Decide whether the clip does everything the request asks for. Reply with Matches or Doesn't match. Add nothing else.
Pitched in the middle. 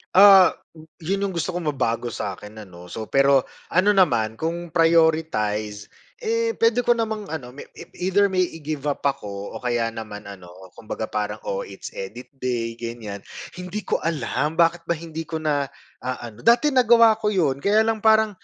Matches